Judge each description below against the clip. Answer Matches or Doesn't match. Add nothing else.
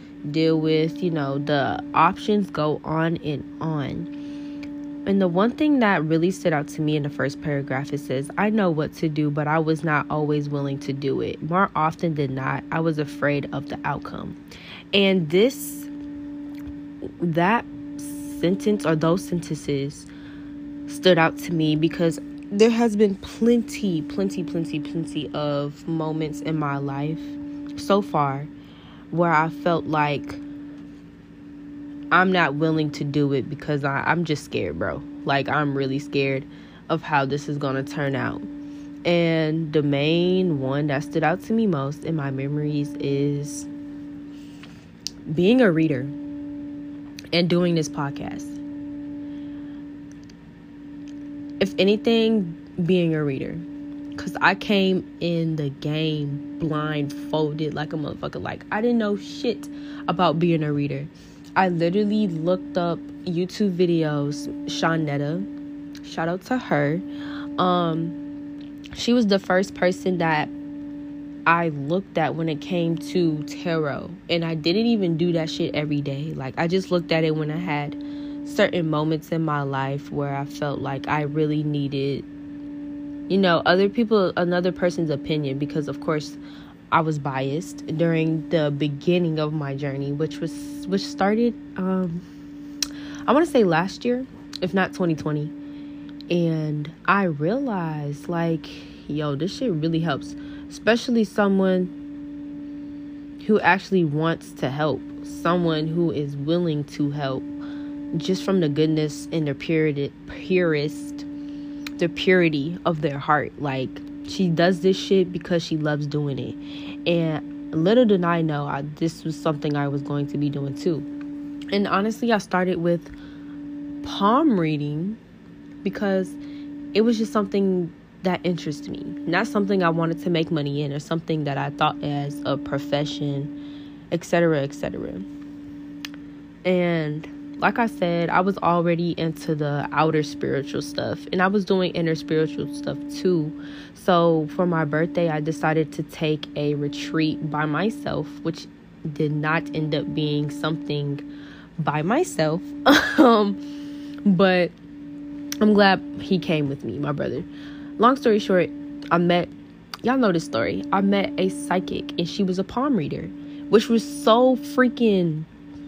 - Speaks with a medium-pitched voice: Matches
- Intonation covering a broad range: Matches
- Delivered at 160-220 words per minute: Doesn't match